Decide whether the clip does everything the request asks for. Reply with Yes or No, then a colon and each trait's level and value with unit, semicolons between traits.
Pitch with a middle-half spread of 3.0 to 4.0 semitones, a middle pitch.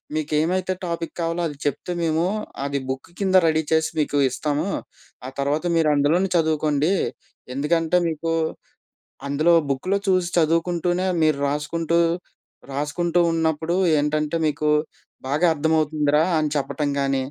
No: narrow, 2.4 semitones; medium, 155 Hz